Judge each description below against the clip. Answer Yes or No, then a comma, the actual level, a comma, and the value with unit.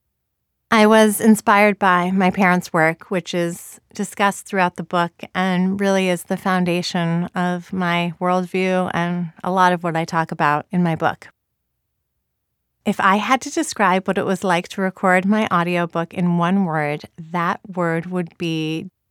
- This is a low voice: No, medium, 180 Hz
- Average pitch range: No, narrow, 2.0 semitones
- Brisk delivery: No, average, 165 wpm